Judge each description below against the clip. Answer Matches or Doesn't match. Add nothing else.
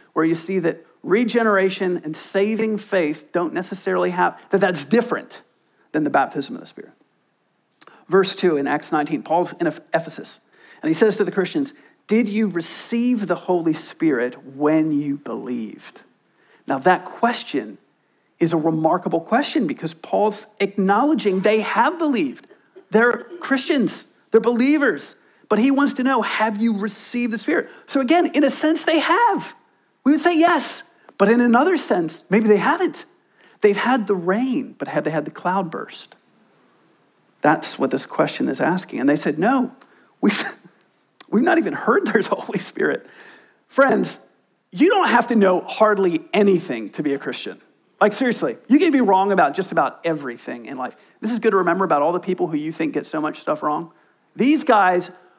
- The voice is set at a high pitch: Matches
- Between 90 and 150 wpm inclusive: Doesn't match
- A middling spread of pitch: Doesn't match